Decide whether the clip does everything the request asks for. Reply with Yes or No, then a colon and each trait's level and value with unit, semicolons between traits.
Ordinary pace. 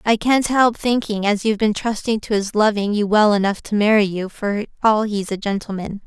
No: fast, 220 wpm